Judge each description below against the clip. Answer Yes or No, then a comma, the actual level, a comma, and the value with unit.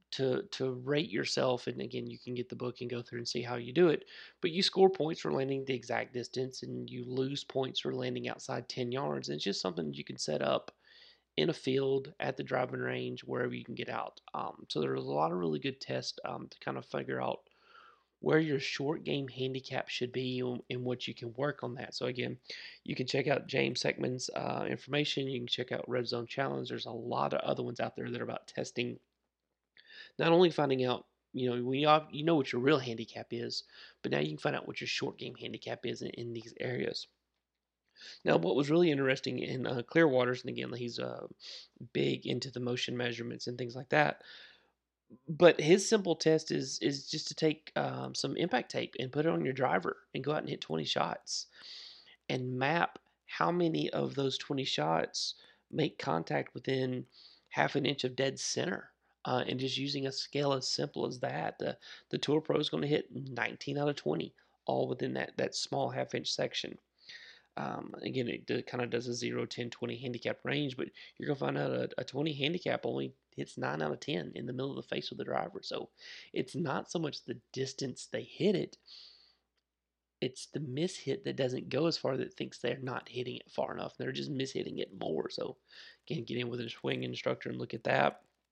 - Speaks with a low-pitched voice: Yes, low, 125 Hz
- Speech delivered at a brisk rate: Yes, fast, 220 wpm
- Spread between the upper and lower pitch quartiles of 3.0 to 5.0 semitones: Yes, average, 3.8 semitones